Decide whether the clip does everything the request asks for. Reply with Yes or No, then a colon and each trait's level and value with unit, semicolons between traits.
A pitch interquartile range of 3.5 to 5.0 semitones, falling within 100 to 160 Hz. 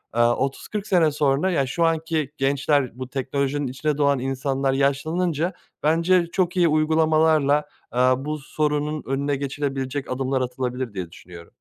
No: average, 2.8 semitones; medium, 140 Hz